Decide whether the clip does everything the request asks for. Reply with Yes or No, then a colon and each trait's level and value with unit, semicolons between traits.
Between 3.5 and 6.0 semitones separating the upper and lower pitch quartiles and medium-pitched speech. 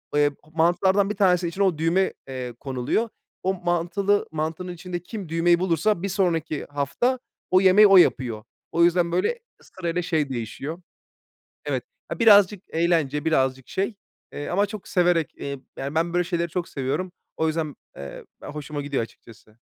Yes: average, 4.1 semitones; medium, 170 Hz